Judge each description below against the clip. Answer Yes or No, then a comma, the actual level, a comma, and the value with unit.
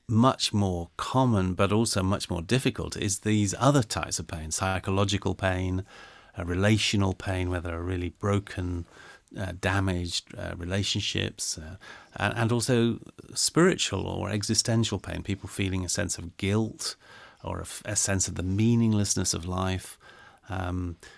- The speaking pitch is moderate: No, very low, 95 Hz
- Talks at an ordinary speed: Yes, average, 150 wpm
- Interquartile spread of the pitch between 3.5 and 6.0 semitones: No, narrow, 2.5 semitones